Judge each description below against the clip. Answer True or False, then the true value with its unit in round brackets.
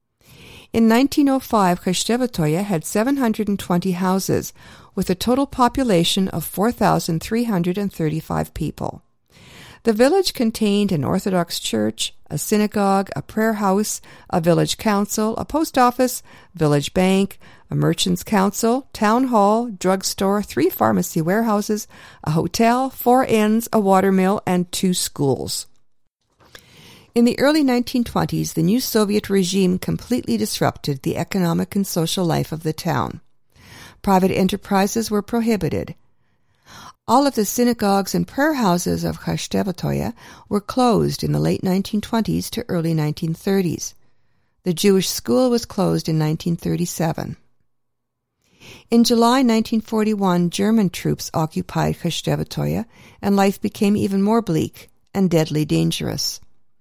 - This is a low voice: False (195 Hz)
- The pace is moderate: False (120 wpm)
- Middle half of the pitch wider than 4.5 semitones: True (5.0 semitones)